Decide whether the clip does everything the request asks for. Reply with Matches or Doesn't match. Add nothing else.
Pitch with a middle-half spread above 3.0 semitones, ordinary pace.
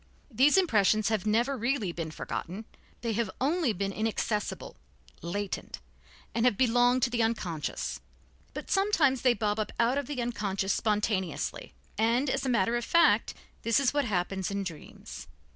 Matches